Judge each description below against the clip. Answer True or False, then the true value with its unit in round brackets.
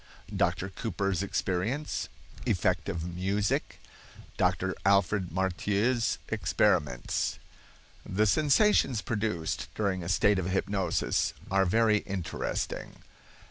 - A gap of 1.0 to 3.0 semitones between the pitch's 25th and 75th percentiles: True (2.7 semitones)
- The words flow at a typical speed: False (85 wpm)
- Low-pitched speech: True (100 Hz)